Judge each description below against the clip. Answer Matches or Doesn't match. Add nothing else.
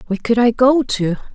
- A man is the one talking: Doesn't match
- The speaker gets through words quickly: Matches